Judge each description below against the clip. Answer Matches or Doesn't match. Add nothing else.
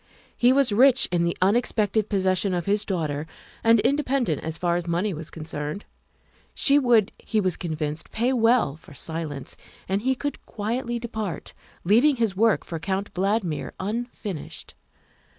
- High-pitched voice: Matches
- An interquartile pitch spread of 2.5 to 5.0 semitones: Doesn't match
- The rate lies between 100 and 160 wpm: Matches